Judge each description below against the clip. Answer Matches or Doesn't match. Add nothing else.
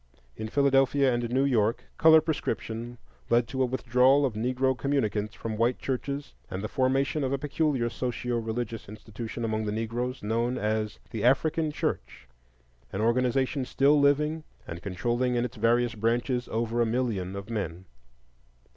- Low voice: Matches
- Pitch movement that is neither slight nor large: Matches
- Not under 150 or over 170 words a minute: Matches